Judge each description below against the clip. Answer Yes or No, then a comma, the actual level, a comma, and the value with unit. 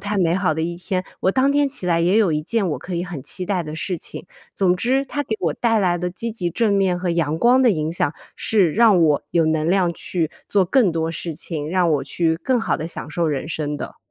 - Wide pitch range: No, average, 4.1 semitones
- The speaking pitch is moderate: Yes, medium, 180 Hz